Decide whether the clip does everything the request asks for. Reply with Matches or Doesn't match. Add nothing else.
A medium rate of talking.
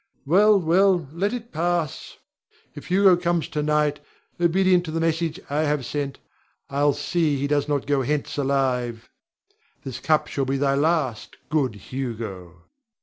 Matches